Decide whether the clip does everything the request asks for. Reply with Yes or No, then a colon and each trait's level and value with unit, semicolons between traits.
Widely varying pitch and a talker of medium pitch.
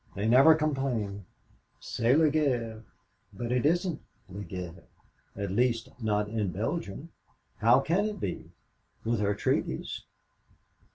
No: wide, 6.4 semitones; low, 115 Hz